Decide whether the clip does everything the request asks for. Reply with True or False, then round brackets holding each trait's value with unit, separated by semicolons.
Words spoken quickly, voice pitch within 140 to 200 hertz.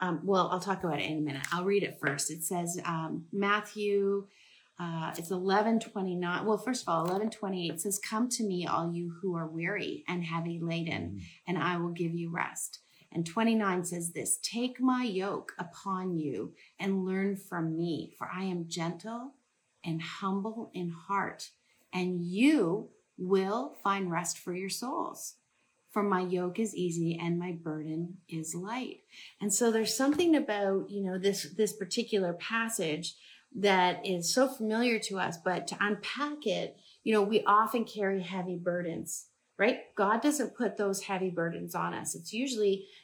False (170 wpm; 190 Hz)